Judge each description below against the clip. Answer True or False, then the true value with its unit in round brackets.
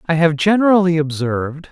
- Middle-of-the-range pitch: True (165 Hz)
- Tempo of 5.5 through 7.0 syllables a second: True (5.7 syllables/s)